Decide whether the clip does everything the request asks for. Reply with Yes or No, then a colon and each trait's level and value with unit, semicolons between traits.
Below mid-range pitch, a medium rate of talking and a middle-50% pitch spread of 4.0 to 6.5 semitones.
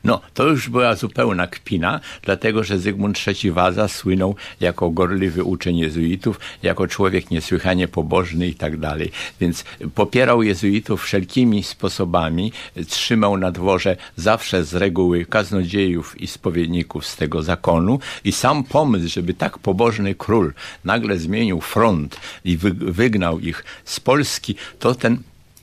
No: very low, 95 Hz; average, 135 wpm; average, 2.9 semitones